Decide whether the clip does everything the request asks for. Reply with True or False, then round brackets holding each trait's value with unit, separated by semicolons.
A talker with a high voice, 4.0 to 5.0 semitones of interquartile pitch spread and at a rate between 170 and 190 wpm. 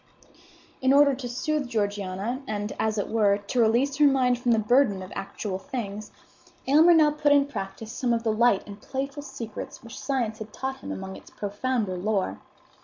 True (235 Hz; 4.6 semitones; 185 wpm)